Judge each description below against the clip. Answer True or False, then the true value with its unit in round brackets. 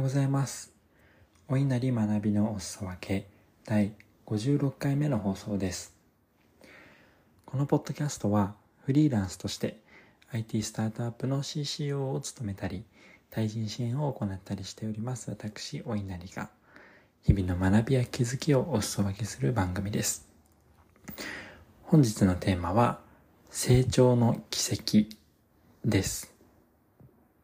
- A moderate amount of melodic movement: True (4.5 semitones)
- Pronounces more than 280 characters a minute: False (240 characters per minute)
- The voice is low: True (105 Hz)